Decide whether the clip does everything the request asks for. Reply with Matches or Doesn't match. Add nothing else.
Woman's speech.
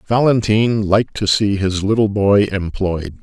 Doesn't match